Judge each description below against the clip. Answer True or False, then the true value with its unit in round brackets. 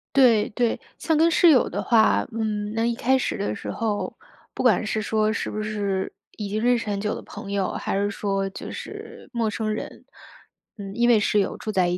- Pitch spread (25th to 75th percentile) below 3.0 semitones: True (2.4 semitones)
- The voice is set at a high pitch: True (215 Hz)